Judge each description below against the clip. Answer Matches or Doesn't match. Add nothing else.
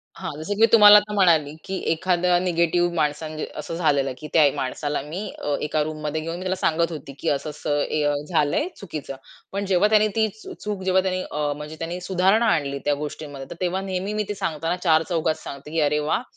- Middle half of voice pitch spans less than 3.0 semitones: Doesn't match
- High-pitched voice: Doesn't match